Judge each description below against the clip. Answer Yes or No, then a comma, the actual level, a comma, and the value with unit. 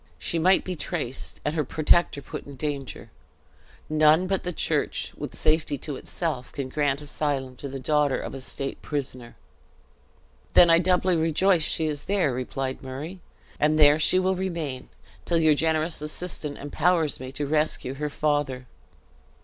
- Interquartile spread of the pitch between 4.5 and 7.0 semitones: No, average, 3.2 semitones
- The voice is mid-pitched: Yes, medium, 150 Hz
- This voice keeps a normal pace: Yes, average, 160 wpm